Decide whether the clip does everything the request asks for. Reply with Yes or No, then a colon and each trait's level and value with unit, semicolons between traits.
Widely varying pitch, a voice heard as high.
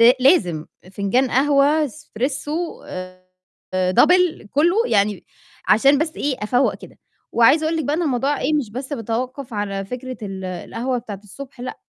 Yes: wide, 5.7 semitones; very high, 255 Hz